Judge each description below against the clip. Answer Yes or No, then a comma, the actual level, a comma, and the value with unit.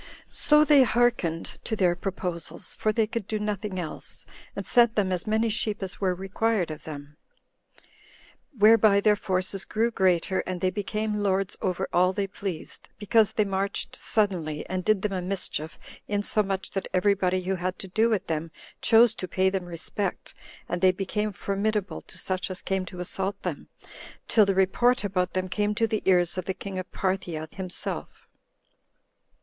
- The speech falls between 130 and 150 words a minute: No, average, 175 wpm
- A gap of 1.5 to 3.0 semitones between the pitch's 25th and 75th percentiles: Yes, narrow, 2.5 semitones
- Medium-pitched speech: No, high, 195 Hz